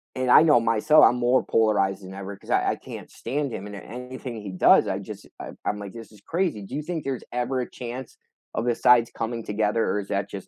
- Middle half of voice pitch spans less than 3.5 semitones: No, average, 3.8 semitones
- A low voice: Yes, low, 115 Hz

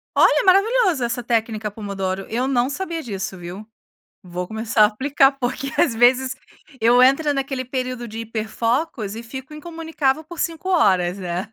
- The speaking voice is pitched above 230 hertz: Yes, high, 245 Hz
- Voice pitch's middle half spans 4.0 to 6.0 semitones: Yes, average, 4.7 semitones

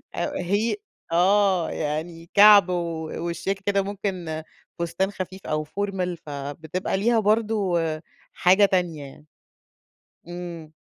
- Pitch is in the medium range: Yes, medium, 180 Hz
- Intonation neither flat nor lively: Yes, average, 3.3 semitones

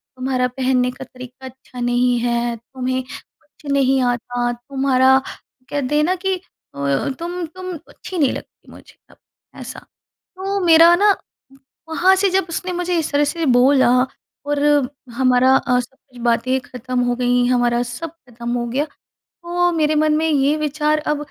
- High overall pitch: Yes, very high, 265 Hz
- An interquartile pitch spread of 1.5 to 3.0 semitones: No, average, 4.5 semitones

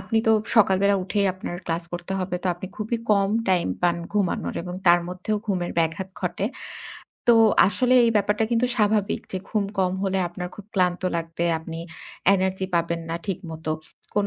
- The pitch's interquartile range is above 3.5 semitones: No, average, 2.8 semitones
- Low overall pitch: No, high, 190 Hz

